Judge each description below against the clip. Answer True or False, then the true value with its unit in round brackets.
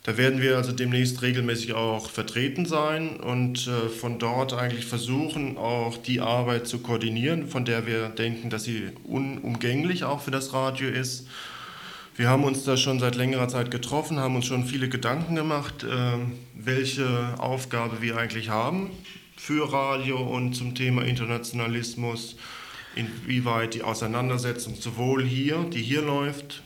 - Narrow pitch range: True (2.2 semitones)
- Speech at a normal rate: True (150 wpm)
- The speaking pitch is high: False (125 Hz)